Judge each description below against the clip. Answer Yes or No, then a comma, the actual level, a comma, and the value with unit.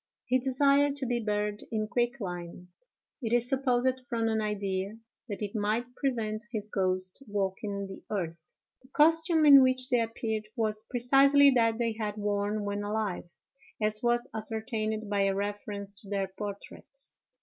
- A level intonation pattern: No, average, 3.4 semitones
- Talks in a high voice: Yes, high, 220 Hz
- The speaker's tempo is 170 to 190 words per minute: No, average, 150 wpm